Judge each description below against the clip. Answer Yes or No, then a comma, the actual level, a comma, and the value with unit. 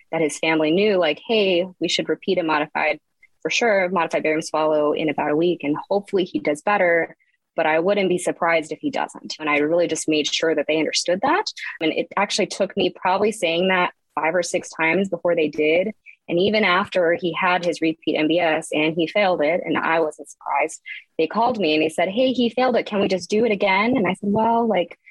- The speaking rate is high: Yes, fast, 225 wpm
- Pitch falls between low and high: Yes, medium, 175 Hz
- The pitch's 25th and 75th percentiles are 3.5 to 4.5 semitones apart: Yes, average, 3.9 semitones